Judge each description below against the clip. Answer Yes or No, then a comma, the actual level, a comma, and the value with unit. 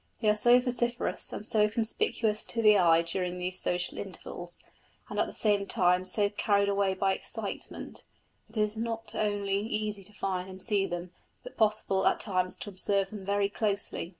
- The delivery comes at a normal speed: Yes, average, 185 wpm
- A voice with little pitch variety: Yes, narrow, 2.3 semitones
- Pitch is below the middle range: No, high, 200 Hz